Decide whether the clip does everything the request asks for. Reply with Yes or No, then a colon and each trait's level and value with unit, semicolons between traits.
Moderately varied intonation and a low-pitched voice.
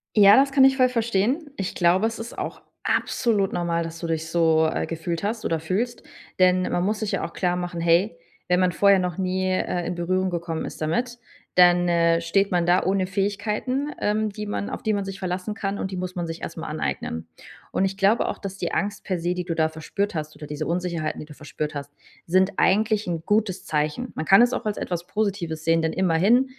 No: average, 3.5 semitones; medium, 185 Hz